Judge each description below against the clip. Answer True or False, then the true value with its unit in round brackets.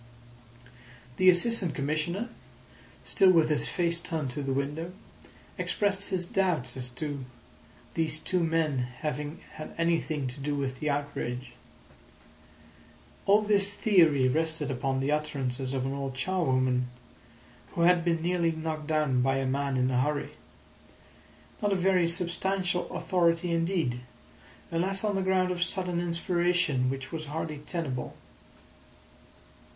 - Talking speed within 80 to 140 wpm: True (135 wpm)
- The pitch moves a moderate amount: True (4.5 semitones)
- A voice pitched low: False (160 Hz)